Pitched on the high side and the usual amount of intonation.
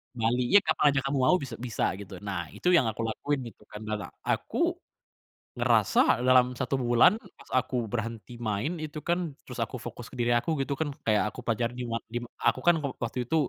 No: low, 125 Hz; average, 3.4 semitones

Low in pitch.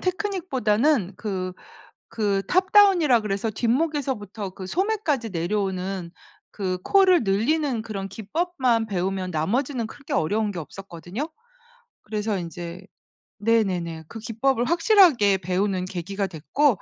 No: high, 215 Hz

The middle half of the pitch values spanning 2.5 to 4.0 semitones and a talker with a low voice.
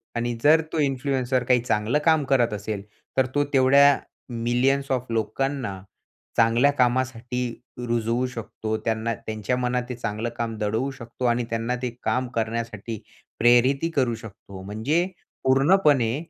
Yes: average, 2.8 semitones; low, 120 Hz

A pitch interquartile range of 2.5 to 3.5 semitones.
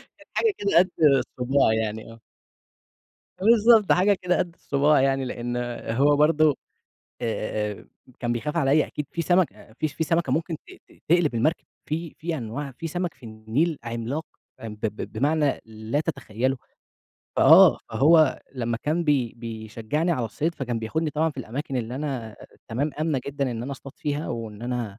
No: wide, 5.4 semitones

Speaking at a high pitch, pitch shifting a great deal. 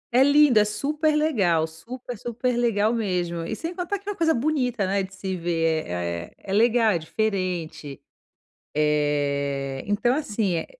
Yes: high, 205 Hz; wide, 7.3 semitones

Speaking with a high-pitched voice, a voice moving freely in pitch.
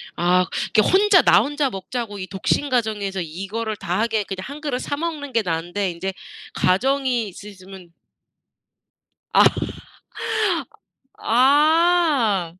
Yes: high, 220 Hz; wide, 6.9 semitones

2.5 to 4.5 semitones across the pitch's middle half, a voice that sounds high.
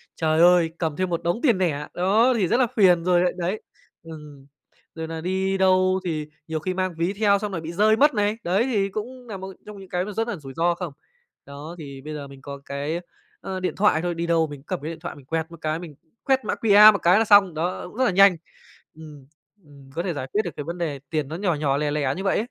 No: average, 4.0 semitones; medium, 175 Hz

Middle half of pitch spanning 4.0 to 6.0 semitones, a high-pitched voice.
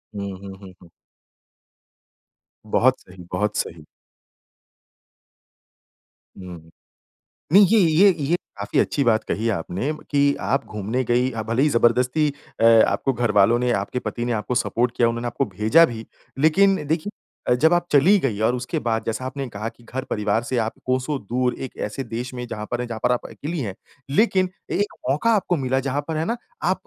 No: average, 4.5 semitones; low, 125 Hz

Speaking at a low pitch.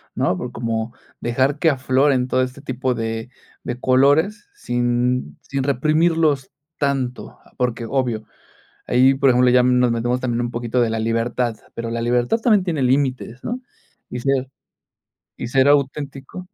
Yes: low, 125 Hz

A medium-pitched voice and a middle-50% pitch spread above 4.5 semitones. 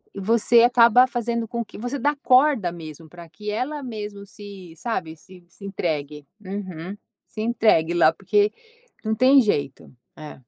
No: high, 205 Hz; wide, 5.5 semitones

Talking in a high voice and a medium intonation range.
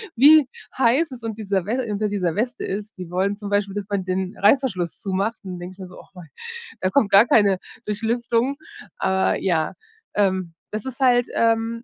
Yes: high, 205 Hz; average, 3.6 semitones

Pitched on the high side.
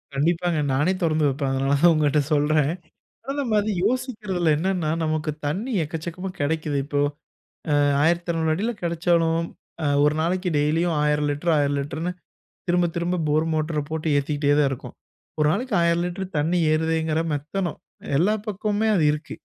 No: medium, 160 Hz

